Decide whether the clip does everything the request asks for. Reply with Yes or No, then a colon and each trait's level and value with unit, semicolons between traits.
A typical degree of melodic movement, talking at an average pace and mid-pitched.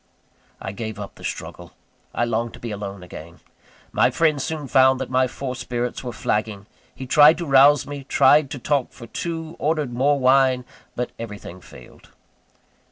No: average, 4.2 semitones; average, 170 wpm; low, 130 Hz